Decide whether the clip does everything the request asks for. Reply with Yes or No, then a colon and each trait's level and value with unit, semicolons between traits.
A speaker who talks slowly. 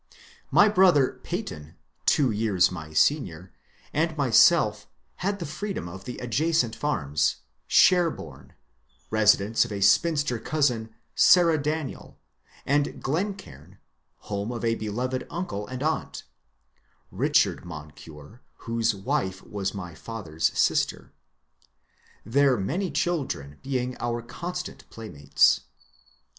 Yes: slow, 115 wpm